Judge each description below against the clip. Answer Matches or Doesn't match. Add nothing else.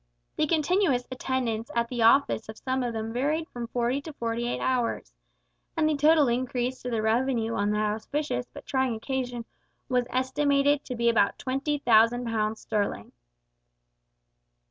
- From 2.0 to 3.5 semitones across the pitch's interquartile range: Matches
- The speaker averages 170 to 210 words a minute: Doesn't match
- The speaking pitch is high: Matches